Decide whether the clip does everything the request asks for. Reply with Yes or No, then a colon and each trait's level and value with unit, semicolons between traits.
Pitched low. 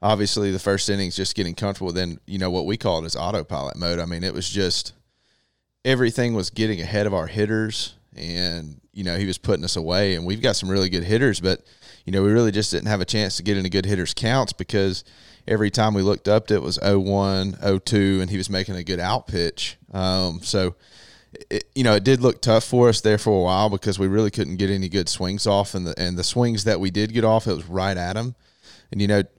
Yes: low, 100 Hz